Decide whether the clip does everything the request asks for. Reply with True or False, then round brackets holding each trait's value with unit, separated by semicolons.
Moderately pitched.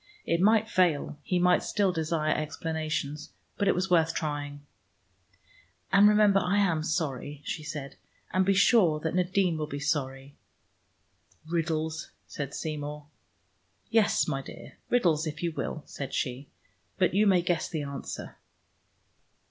True (160 Hz)